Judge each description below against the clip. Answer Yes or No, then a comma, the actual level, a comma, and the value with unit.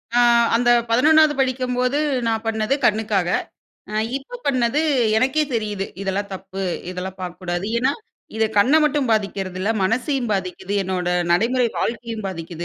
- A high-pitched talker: Yes, high, 220 Hz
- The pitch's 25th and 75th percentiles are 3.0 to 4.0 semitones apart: No, average, 5.0 semitones